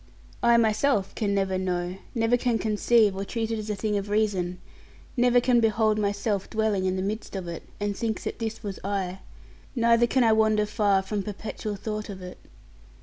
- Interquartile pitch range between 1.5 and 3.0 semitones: Yes, narrow, 2.5 semitones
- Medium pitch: No, high, 210 Hz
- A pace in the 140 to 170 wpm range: No, average, 195 wpm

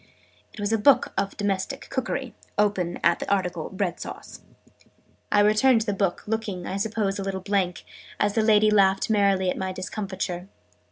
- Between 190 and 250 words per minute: No, average, 170 wpm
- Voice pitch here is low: No, high, 200 Hz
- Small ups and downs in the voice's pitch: Yes, narrow, 2.2 semitones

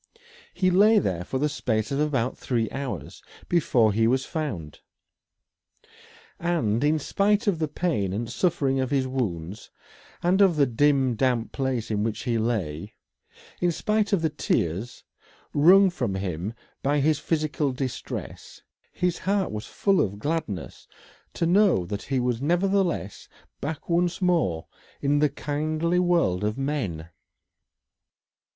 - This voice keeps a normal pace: Yes, average, 145 wpm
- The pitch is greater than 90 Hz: Yes, medium, 140 Hz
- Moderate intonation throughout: No, wide, 7.3 semitones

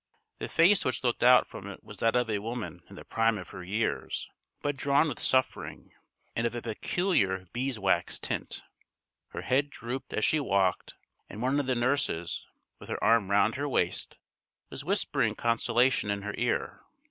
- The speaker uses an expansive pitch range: No, average, 4.4 semitones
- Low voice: Yes, low, 120 Hz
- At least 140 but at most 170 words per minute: No, average, 180 wpm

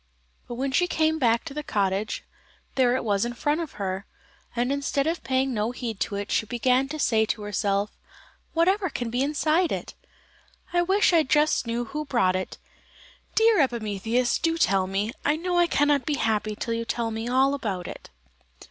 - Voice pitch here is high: Yes, very high, 250 Hz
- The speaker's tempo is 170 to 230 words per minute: Yes, average, 190 wpm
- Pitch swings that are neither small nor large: No, wide, 5.7 semitones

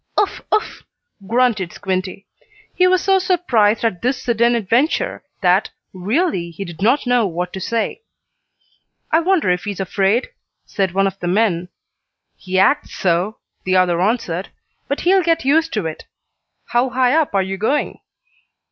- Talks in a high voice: Yes, high, 215 Hz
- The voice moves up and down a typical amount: No, wide, 6.9 semitones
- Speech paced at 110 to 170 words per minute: Yes, average, 155 wpm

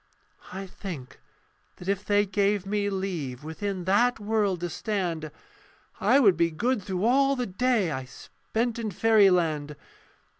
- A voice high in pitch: Yes, high, 195 Hz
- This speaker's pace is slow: No, average, 145 wpm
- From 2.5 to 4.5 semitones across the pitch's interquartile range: Yes, average, 3.8 semitones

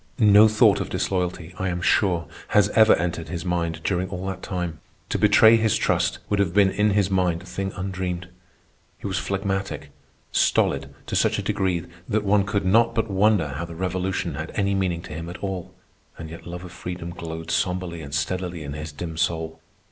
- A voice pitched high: No, very low, 90 Hz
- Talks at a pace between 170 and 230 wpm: Yes, average, 200 wpm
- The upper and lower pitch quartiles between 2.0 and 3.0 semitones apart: Yes, average, 2.7 semitones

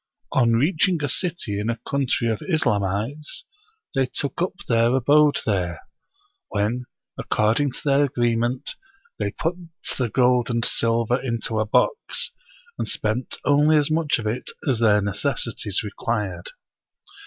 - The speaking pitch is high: No, low, 120 Hz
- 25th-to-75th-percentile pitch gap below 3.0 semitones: No, average, 4.6 semitones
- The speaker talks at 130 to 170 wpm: Yes, average, 140 wpm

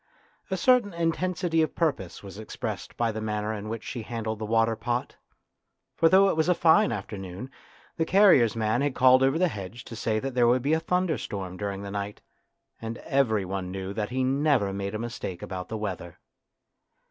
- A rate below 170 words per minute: No, average, 195 wpm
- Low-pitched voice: Yes, low, 115 Hz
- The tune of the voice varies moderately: No, wide, 6.2 semitones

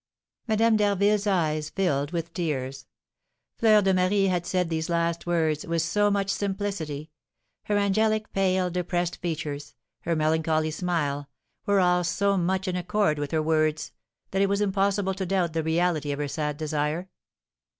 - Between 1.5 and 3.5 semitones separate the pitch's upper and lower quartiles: No, average, 3.9 semitones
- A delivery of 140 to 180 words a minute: Yes, average, 160 wpm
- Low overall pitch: No, medium, 175 Hz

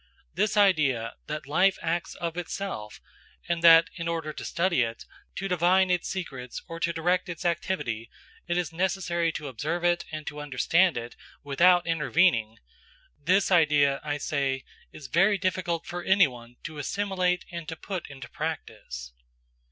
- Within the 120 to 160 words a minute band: Yes, average, 150 wpm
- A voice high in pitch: No, medium, 165 Hz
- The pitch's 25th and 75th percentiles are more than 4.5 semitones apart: No, average, 4.1 semitones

